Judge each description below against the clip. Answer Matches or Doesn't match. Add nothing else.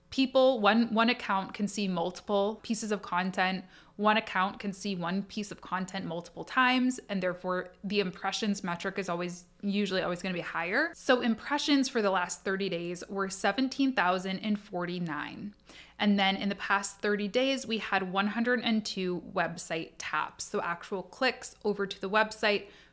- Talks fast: Doesn't match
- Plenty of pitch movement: Doesn't match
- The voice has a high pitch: Matches